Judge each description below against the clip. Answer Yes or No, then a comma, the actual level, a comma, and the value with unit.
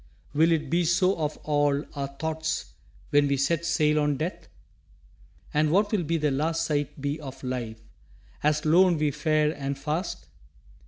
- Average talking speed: Yes, average, 160 wpm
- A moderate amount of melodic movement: No, narrow, 2.3 semitones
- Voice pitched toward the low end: No, medium, 150 Hz